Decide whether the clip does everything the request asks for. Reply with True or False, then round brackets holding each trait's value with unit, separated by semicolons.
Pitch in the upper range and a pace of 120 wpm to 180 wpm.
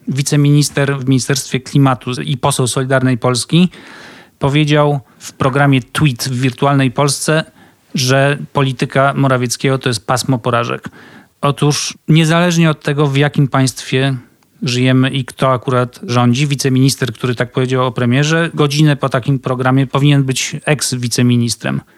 False (135 Hz; 130 wpm)